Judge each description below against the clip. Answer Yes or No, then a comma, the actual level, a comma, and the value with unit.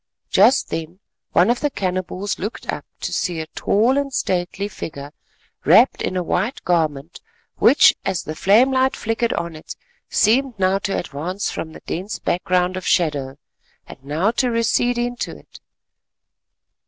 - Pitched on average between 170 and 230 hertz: Yes, medium, 185 Hz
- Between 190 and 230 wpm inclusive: No, average, 155 wpm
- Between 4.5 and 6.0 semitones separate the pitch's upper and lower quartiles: Yes, wide, 5.6 semitones